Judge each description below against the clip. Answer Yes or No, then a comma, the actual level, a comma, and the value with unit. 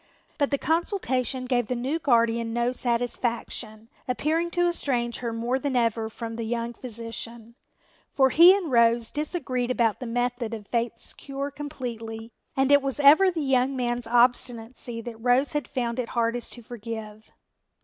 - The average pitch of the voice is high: Yes, high, 245 Hz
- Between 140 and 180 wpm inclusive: Yes, average, 160 wpm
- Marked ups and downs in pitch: No, average, 2.8 semitones